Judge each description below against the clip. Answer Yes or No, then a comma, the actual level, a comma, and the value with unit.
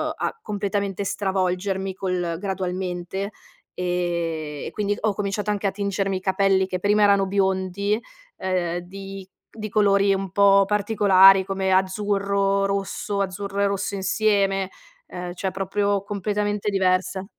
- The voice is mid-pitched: No, high, 195 Hz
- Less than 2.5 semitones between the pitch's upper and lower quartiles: Yes, narrow, 1.3 semitones